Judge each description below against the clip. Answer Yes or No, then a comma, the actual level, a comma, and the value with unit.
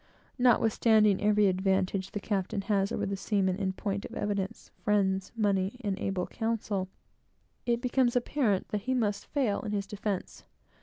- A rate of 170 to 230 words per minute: No, average, 155 wpm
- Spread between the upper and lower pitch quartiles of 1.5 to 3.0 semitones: Yes, narrow, 2.5 semitones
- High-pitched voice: Yes, high, 205 Hz